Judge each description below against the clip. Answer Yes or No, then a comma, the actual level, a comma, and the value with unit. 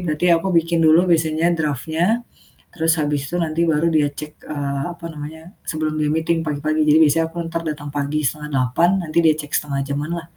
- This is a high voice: No, medium, 155 Hz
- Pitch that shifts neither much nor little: No, narrow, 2.0 semitones